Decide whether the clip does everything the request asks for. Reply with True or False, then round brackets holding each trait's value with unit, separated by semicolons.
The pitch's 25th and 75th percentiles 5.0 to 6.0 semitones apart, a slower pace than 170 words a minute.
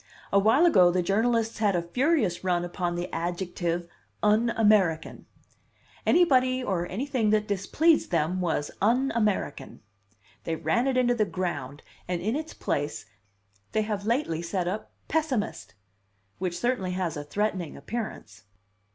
True (5.3 semitones; 145 wpm)